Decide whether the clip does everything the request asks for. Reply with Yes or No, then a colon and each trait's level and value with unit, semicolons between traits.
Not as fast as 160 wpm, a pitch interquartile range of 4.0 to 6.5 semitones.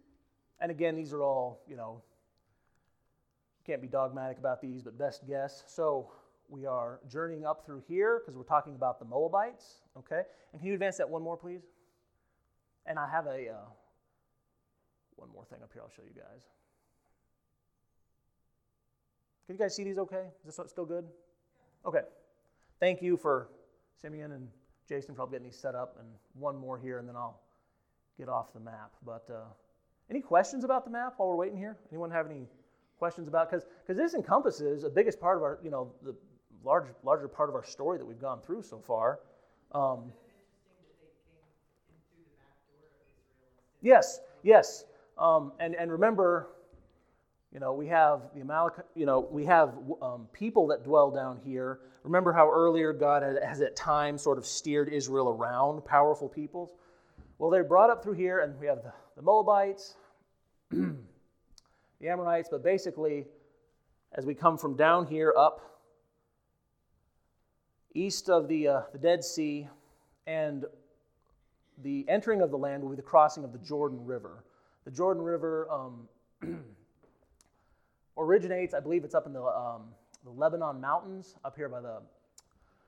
No: average, 165 wpm; average, 4.7 semitones